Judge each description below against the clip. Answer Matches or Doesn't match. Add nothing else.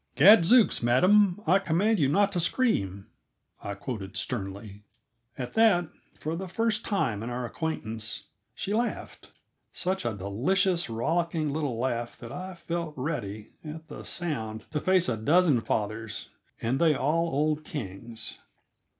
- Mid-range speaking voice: Matches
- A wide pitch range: Matches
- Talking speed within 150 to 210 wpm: Doesn't match